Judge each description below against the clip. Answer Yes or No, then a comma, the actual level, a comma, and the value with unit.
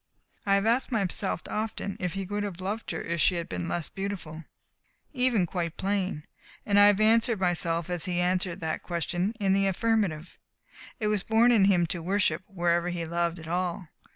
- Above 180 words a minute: Yes, average, 190 wpm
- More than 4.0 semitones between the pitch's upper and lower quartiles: No, average, 3.1 semitones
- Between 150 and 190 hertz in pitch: Yes, medium, 185 Hz